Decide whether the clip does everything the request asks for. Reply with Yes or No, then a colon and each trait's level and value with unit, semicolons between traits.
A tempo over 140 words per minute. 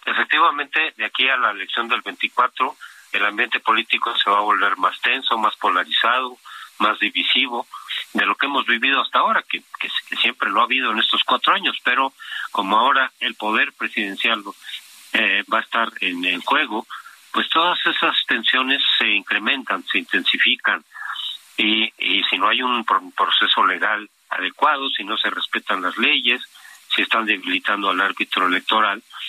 Yes: average, 165 wpm